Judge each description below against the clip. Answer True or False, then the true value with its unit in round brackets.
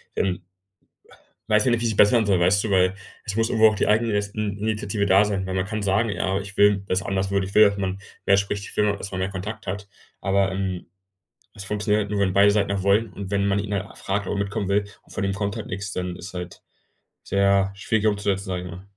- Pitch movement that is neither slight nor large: False (1.3 semitones)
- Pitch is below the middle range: True (100 Hz)